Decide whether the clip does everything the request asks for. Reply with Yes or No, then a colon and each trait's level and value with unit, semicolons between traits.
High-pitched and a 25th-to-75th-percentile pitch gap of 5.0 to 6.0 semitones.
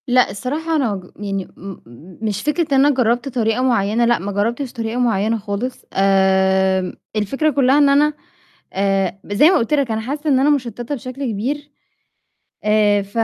Yes: high, 235 Hz; average, 5.3 semitones